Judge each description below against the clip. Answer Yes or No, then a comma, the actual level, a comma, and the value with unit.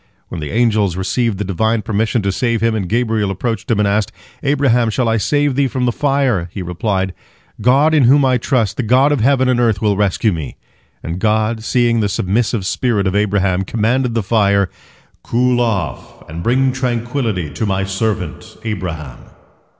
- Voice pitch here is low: Yes, low, 110 Hz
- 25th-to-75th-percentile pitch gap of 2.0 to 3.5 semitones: No, average, 4.1 semitones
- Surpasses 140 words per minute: Yes, average, 180 wpm